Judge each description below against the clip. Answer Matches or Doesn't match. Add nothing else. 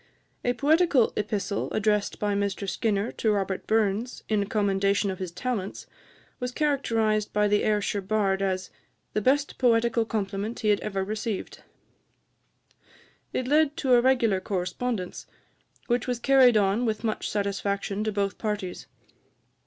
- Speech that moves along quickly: Doesn't match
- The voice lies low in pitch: Doesn't match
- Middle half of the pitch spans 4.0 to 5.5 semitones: Doesn't match